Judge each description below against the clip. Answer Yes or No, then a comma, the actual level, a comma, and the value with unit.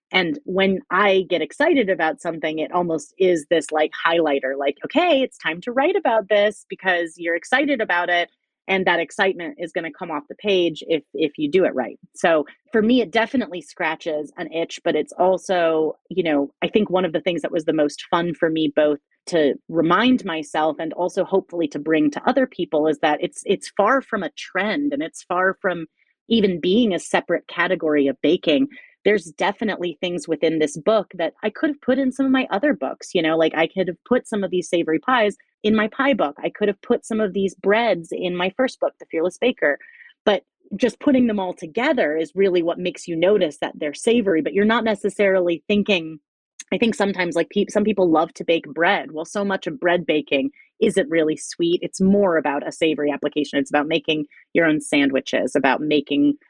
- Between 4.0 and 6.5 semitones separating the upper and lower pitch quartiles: Yes, average, 4.8 semitones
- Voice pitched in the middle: Yes, medium, 180 Hz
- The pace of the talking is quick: Yes, fast, 215 wpm